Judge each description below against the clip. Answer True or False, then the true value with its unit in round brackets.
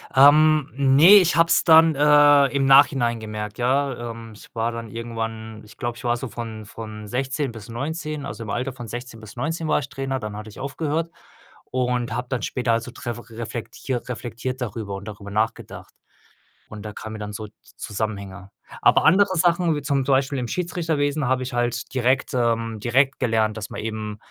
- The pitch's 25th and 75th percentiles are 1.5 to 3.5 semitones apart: False (3.9 semitones)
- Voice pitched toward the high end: False (120 Hz)